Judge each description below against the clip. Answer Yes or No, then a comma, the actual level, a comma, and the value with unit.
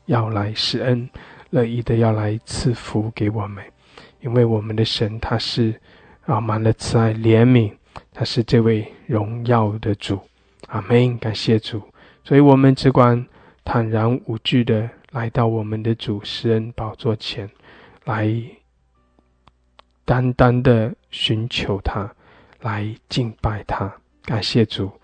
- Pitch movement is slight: Yes, narrow, 1.9 semitones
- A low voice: Yes, low, 115 Hz